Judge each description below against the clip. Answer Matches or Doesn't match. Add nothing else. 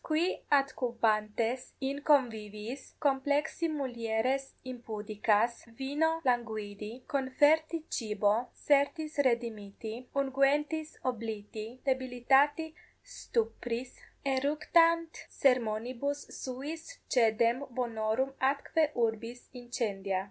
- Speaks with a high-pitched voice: Matches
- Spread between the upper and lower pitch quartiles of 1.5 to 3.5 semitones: Doesn't match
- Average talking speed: Doesn't match